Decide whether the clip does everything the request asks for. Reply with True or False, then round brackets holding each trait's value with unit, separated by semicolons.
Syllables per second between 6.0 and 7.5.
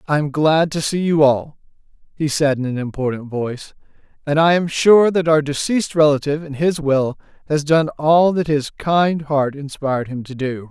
False (5.0 syllables/s)